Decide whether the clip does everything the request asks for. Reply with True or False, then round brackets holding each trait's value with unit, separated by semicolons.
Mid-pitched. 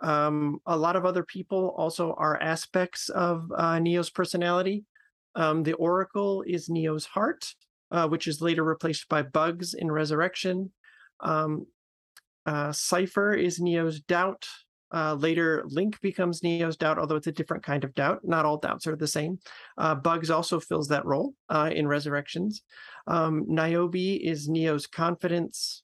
True (165 Hz)